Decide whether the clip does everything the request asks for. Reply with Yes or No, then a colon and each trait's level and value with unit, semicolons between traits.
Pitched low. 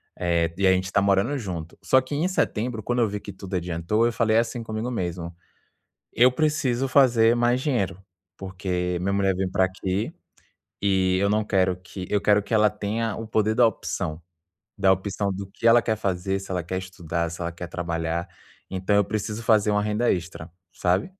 Yes: low, 100 Hz